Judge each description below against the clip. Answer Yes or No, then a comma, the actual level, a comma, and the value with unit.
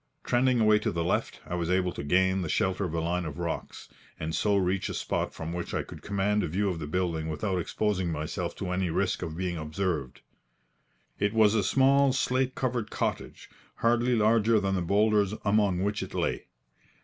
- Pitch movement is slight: No, average, 3.8 semitones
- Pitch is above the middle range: No, very low, 95 Hz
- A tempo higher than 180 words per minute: Yes, average, 200 wpm